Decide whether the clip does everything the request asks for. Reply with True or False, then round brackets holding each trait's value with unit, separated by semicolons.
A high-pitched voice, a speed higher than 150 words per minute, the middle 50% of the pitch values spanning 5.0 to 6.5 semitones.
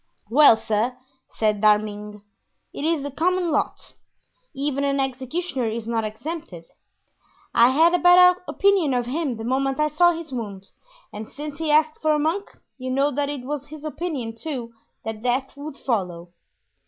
True (275 Hz; 165 wpm; 5.3 semitones)